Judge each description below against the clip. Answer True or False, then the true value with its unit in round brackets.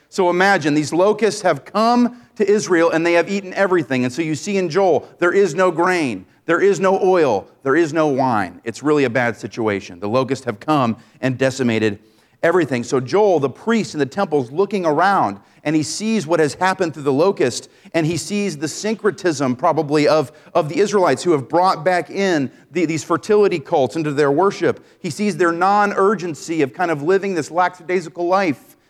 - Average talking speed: True (195 wpm)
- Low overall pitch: False (170 Hz)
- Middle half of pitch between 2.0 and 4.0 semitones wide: False (4.9 semitones)